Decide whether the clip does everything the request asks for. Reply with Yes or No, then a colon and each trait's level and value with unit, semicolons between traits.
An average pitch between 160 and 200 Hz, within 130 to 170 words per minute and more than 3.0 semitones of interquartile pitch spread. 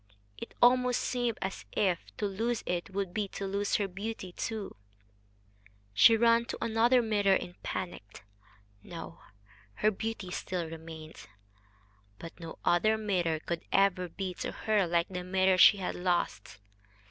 Yes: high, 190 Hz; average, 145 wpm; average, 3.8 semitones